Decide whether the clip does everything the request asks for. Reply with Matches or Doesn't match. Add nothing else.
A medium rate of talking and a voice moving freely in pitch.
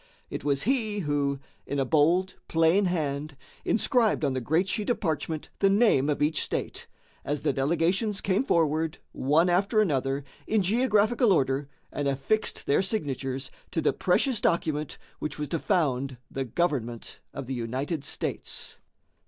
Matches